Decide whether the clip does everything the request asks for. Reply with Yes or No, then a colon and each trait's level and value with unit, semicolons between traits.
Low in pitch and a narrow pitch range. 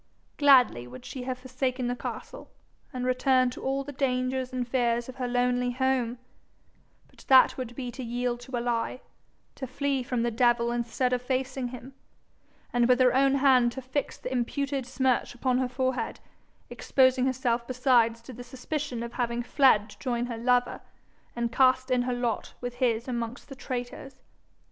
No: very high, 250 Hz; narrow, 1.5 semitones